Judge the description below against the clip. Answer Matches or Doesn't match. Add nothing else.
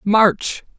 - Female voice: Doesn't match